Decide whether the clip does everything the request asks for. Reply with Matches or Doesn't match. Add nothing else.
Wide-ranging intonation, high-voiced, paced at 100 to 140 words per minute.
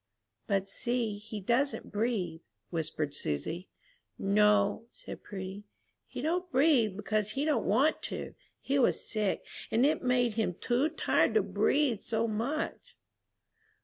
Doesn't match